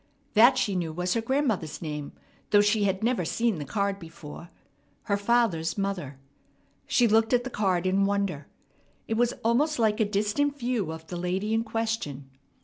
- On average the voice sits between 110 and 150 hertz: No, high, 205 Hz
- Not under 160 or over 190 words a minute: Yes, average, 175 wpm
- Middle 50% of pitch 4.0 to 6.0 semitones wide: Yes, average, 4.6 semitones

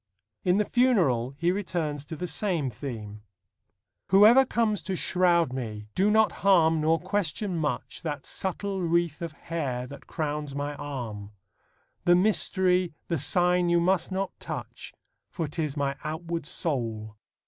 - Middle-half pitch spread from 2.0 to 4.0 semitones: No, average, 4.7 semitones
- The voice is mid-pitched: Yes, medium, 165 Hz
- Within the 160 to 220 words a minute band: No, average, 145 wpm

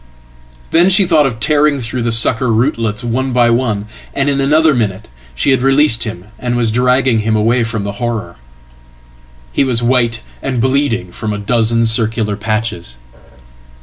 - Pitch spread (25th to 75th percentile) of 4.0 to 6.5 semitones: No, average, 3.5 semitones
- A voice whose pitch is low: Yes, low, 115 Hz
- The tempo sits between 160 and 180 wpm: No, average, 150 wpm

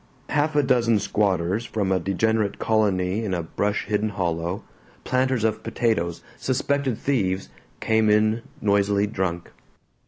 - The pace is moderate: No, slow, 130 wpm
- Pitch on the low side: Yes, low, 105 Hz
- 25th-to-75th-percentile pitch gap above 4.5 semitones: No, average, 3.3 semitones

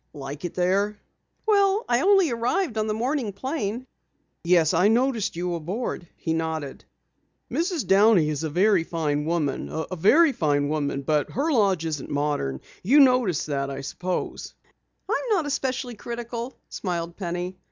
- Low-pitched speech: No, high, 190 Hz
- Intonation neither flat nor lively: No, wide, 7.8 semitones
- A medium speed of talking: Yes, average, 150 wpm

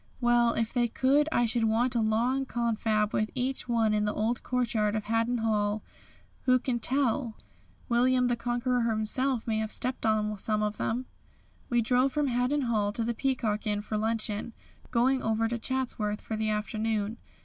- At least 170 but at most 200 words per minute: Yes, average, 180 wpm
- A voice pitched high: Yes, high, 230 Hz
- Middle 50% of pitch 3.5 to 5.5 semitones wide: No, narrow, 2.4 semitones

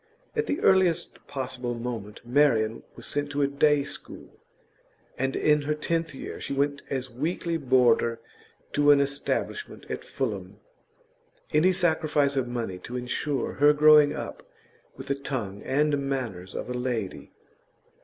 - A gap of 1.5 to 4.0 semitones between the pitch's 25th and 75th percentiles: Yes, average, 3.3 semitones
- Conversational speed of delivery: Yes, average, 145 wpm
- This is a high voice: No, medium, 140 Hz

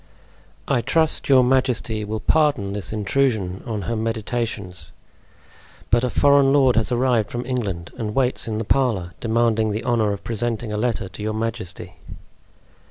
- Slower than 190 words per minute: Yes, average, 160 wpm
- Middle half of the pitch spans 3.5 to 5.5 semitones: No, average, 2.9 semitones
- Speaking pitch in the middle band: No, low, 115 Hz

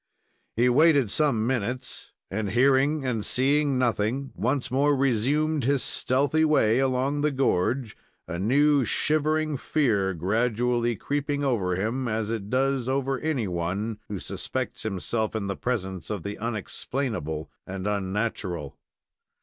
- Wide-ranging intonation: No, average, 4.9 semitones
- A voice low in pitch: Yes, low, 125 Hz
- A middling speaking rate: No, slow, 130 wpm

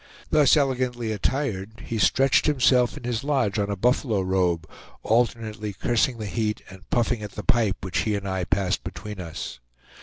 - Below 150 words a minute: No, average, 175 wpm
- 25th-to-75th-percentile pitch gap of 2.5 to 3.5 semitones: No, average, 4.0 semitones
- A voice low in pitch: Yes, low, 110 Hz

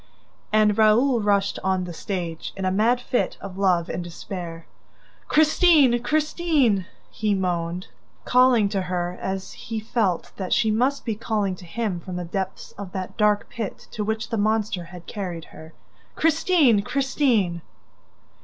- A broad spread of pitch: No, average, 4.3 semitones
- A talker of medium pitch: No, high, 205 Hz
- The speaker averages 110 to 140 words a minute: No, average, 155 wpm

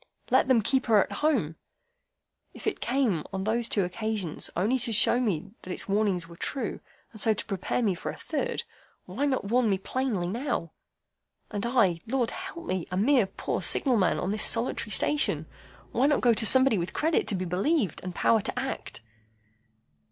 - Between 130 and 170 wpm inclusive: No, average, 190 wpm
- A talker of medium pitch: No, high, 220 Hz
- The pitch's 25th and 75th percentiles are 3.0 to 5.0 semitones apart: No, wide, 5.4 semitones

